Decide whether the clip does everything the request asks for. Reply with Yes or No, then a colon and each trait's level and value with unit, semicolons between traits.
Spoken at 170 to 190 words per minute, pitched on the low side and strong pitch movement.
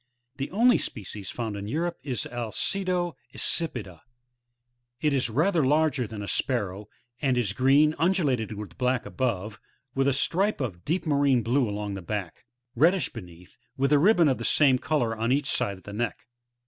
Yes: average, 175 wpm; low, 130 Hz; wide, 6.1 semitones